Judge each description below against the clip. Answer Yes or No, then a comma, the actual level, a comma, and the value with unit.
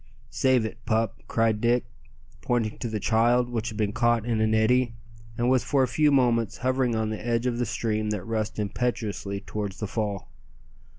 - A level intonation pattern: Yes, narrow, 2.1 semitones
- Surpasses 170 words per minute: Yes, average, 190 wpm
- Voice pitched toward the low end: Yes, low, 115 Hz